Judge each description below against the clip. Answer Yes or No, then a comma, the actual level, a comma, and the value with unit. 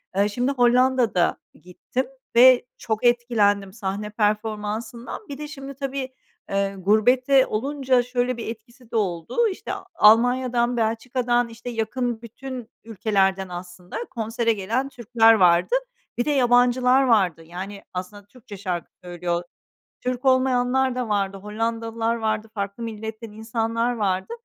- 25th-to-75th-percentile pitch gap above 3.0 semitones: Yes, average, 3.4 semitones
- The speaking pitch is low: No, high, 230 Hz